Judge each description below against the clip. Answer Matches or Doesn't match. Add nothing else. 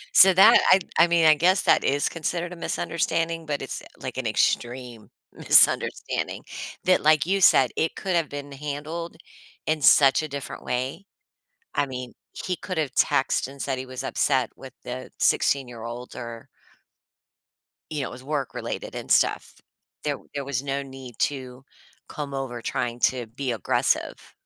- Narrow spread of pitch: Doesn't match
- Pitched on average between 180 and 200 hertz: Doesn't match